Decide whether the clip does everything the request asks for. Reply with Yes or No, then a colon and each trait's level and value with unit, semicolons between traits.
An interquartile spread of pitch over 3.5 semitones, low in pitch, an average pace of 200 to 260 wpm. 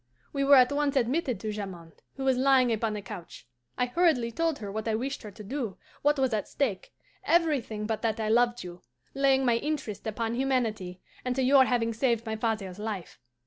No: average, 4.0 semitones; high, 235 Hz; fast, 205 wpm